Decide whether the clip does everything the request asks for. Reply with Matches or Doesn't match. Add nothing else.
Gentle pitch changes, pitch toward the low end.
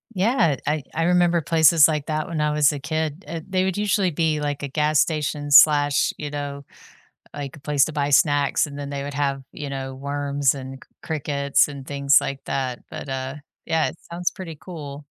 Doesn't match